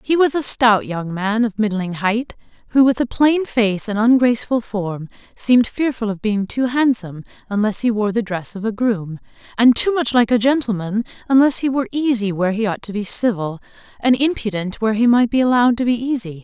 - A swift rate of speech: Yes, fast, 210 wpm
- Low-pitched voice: No, high, 225 Hz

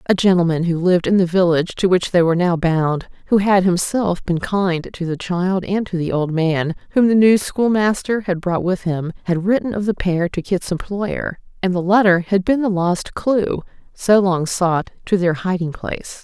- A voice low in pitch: No, medium, 185 Hz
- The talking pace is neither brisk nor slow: No, fast, 210 wpm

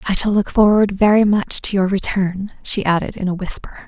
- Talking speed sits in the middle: No, fast, 215 wpm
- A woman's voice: Yes, female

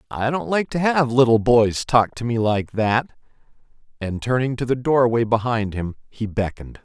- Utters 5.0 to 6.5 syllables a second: No, 4.8 syllables/s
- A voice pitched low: Yes, low, 120 Hz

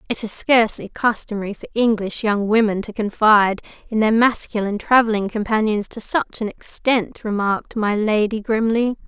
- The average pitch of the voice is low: No, high, 220 Hz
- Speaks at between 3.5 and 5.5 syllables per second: Yes, 5.2 syllables/s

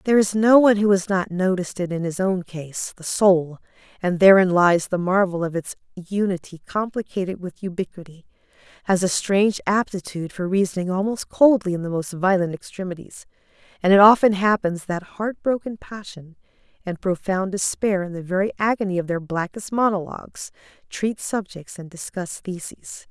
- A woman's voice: Yes, female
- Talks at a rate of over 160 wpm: No, average, 155 wpm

